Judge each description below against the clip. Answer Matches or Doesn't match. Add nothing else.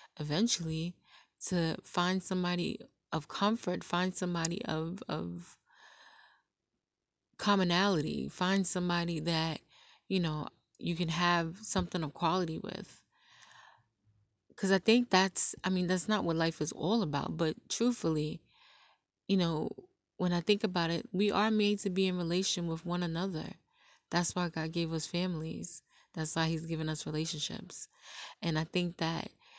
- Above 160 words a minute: Doesn't match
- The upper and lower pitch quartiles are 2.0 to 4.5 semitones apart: Matches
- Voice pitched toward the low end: Doesn't match